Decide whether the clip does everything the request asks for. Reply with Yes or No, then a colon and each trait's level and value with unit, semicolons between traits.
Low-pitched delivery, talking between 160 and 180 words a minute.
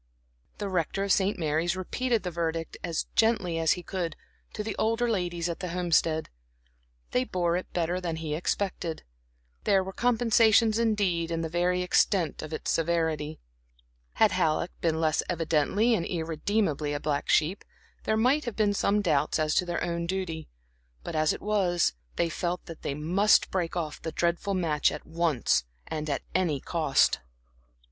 No: medium, 175 Hz; average, 170 wpm